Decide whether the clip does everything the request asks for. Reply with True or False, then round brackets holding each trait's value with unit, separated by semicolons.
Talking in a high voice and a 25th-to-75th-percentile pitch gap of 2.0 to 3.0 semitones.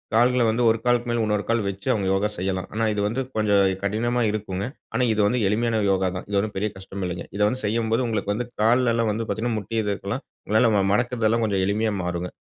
False (110 Hz; 2.6 semitones)